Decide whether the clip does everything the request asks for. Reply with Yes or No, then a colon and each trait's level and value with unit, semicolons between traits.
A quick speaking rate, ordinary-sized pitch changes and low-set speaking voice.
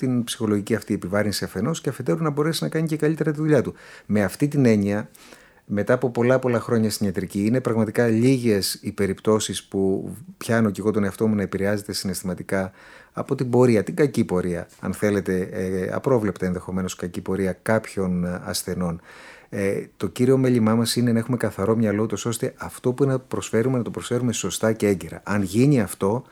Yes: fast, 190 wpm; average, 4.1 semitones; low, 110 Hz